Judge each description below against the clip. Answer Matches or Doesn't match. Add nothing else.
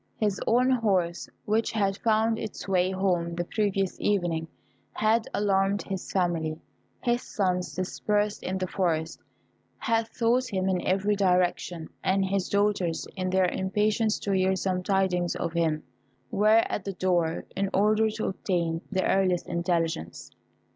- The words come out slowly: Doesn't match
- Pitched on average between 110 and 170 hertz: Doesn't match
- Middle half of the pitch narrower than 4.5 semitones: Matches